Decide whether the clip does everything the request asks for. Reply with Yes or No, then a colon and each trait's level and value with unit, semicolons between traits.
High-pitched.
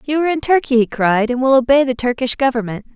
Yes: very high, 255 Hz